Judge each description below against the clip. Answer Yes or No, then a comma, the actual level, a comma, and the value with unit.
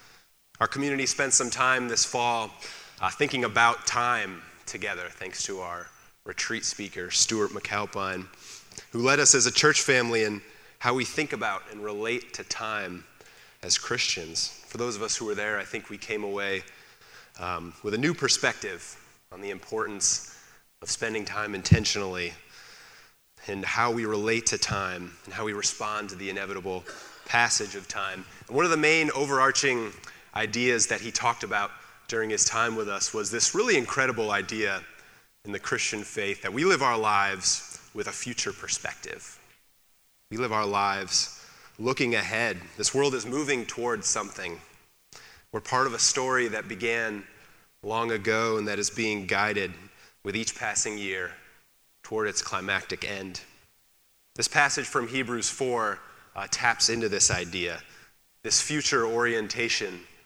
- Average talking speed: Yes, average, 155 wpm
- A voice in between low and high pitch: No, low, 110 Hz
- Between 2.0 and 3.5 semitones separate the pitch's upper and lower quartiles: Yes, average, 3.1 semitones